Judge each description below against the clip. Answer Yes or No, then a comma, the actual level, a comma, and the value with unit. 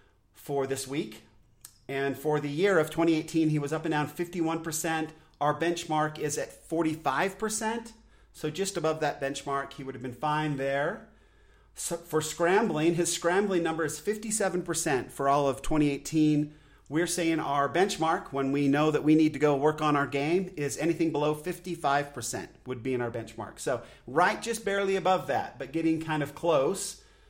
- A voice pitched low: No, medium, 155 Hz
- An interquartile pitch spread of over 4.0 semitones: No, average, 3.2 semitones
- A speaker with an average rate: Yes, average, 175 wpm